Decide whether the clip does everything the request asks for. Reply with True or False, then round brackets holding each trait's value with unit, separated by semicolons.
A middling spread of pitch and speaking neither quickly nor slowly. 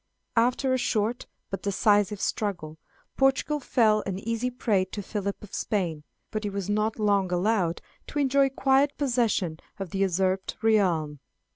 True (3.9 semitones; 150 wpm)